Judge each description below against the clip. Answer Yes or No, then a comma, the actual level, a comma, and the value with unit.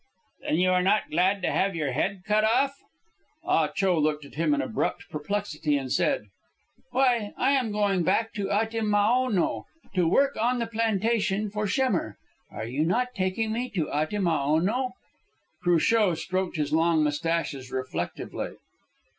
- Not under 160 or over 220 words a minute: No, average, 150 wpm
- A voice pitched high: Yes, high, 195 Hz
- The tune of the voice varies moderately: No, wide, 5.7 semitones